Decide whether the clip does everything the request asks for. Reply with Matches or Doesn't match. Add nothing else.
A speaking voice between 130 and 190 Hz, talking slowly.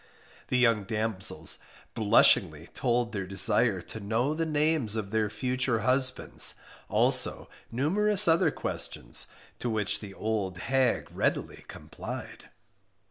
Doesn't match